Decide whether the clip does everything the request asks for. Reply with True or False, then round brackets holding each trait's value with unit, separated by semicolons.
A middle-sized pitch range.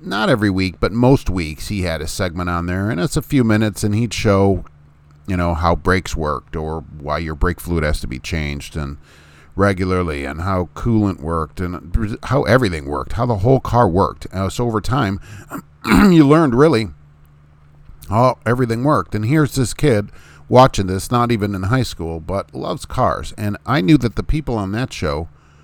False (6.9 semitones)